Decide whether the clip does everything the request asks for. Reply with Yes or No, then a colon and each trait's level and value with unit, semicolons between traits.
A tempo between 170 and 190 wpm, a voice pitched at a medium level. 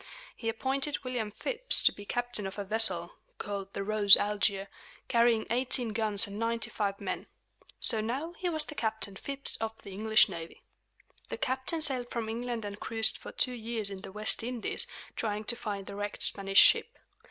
No: average, 180 wpm; high, 220 Hz